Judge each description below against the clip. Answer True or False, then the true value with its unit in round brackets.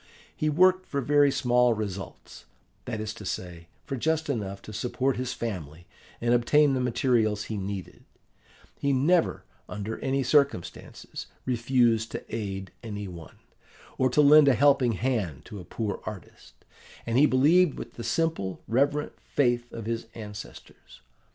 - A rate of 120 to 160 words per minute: True (150 wpm)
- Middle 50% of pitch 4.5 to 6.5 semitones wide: True (5.1 semitones)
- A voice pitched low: True (120 Hz)